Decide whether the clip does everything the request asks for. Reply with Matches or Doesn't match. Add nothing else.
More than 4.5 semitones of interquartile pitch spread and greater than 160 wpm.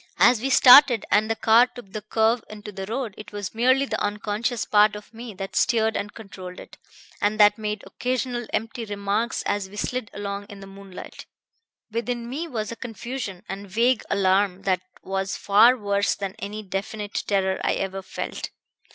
Doesn't match